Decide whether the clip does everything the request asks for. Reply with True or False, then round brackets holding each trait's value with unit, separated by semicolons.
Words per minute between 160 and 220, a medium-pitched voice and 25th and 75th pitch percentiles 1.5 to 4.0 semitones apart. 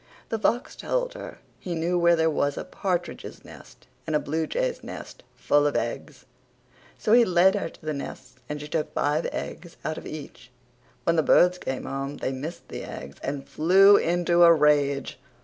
True (185 wpm; 160 Hz; 3.7 semitones)